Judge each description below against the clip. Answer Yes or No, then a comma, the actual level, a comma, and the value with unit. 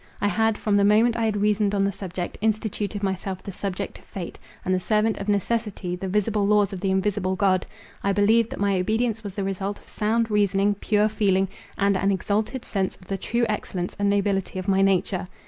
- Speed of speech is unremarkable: No, fast, 210 wpm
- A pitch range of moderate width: No, narrow, 1.7 semitones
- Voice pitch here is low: No, high, 200 Hz